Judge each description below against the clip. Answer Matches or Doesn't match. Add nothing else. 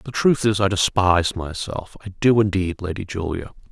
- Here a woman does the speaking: Doesn't match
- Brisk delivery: Doesn't match